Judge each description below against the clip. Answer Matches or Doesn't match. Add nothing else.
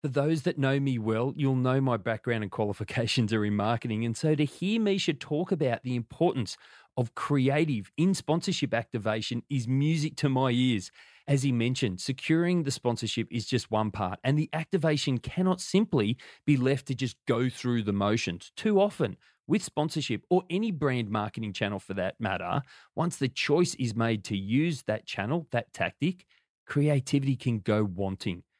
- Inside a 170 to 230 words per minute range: Matches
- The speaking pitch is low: Matches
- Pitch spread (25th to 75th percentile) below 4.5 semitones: Doesn't match